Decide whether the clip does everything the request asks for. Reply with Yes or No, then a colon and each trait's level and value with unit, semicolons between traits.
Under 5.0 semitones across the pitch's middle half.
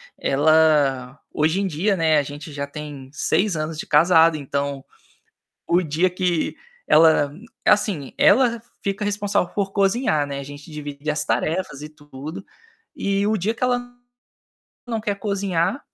No: average, 5.3 semitones